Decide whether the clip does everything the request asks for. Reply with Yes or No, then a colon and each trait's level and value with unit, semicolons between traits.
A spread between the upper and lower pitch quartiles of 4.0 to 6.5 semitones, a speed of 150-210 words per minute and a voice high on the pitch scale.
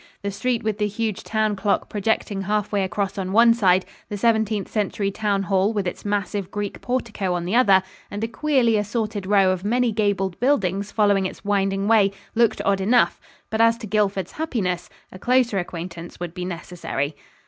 No: narrow, 2.6 semitones; average, 185 wpm; high, 205 Hz